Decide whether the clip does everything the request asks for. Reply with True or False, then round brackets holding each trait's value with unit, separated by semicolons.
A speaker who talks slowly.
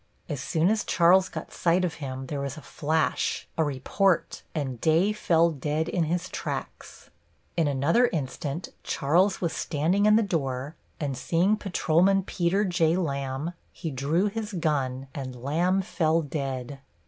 False (155 wpm)